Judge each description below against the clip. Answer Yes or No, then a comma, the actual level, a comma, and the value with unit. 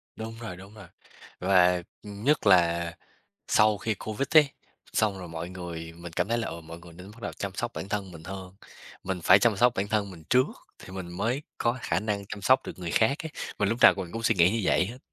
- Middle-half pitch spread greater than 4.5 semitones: No, average, 4.0 semitones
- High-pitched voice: No, low, 100 Hz